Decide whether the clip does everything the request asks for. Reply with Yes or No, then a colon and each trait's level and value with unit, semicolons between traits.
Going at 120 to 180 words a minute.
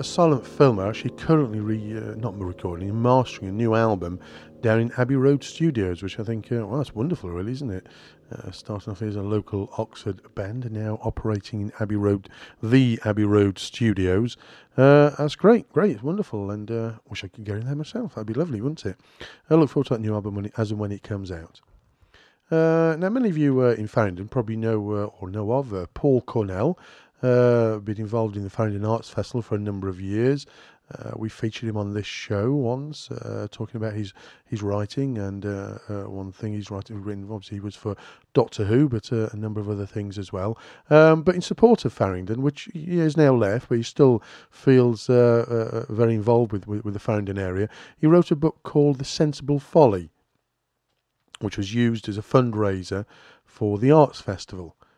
No: fast, 205 wpm